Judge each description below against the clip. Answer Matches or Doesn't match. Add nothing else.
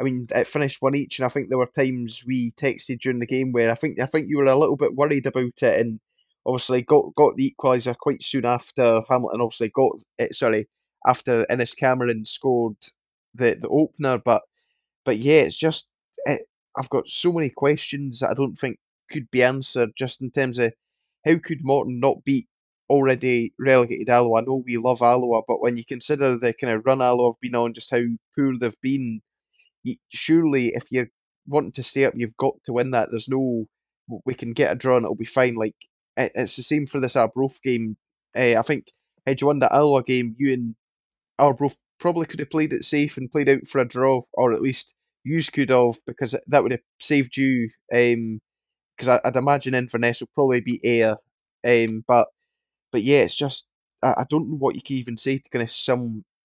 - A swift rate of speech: Matches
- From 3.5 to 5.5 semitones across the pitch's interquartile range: Doesn't match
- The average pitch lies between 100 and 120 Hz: Doesn't match